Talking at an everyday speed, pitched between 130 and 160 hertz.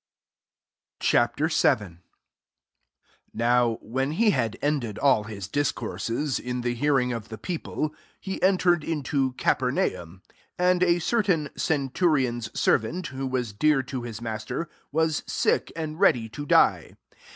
Yes: average, 150 wpm; low, 135 Hz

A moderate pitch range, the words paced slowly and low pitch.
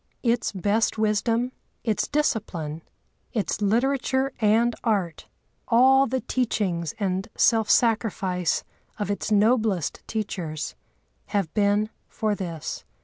No: average, 3.4 semitones; slow, 105 wpm; high, 215 Hz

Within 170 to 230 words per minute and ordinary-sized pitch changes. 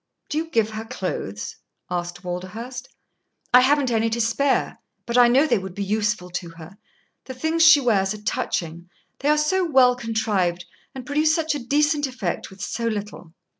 No: average, 180 wpm; wide, 6.5 semitones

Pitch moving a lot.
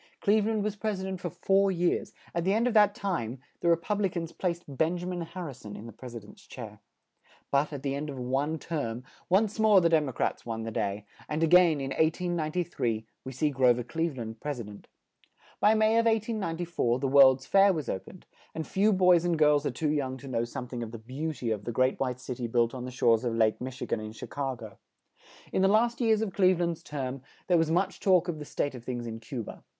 Yes: wide, 6.6 semitones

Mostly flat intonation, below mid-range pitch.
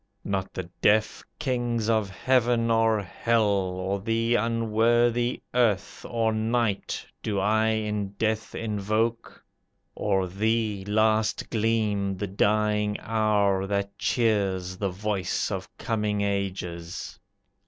Yes: narrow, 2.3 semitones; low, 105 Hz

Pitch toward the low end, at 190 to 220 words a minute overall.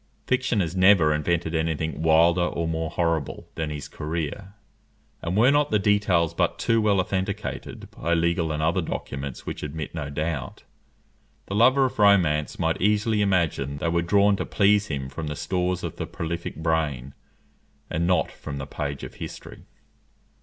No: very low, 85 Hz; average, 170 wpm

